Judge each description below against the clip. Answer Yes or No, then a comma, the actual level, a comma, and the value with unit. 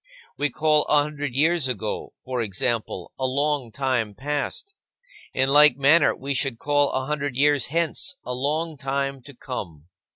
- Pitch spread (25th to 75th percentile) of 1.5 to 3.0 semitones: Yes, average, 2.7 semitones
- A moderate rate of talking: Yes, average, 160 wpm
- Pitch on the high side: No, medium, 140 Hz